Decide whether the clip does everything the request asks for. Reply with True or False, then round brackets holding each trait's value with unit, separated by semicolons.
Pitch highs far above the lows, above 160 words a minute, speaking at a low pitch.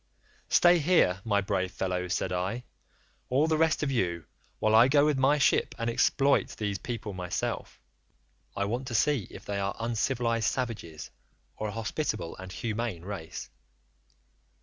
False (5.9 semitones; 155 wpm; 110 Hz)